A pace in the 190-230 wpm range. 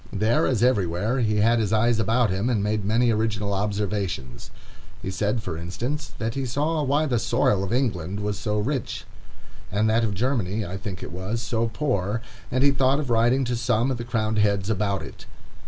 Yes: average, 200 wpm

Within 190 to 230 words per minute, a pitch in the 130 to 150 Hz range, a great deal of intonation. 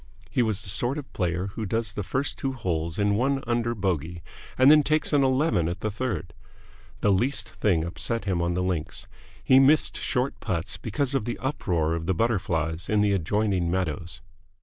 No: average, 195 wpm; low, 105 Hz; wide, 6.2 semitones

